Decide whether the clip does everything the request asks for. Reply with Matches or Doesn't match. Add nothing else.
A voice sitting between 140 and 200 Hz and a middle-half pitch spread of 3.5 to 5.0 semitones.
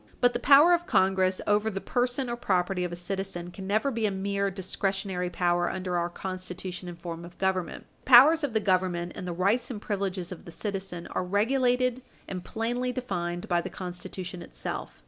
Matches